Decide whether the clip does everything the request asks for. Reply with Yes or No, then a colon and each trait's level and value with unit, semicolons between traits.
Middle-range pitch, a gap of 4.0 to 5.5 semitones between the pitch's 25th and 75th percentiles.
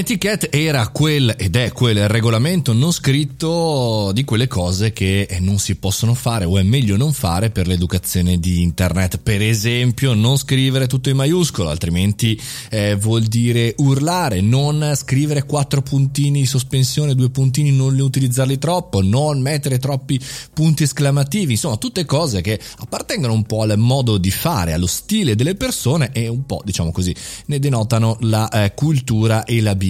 No: low, 120 Hz; average, 5.2 semitones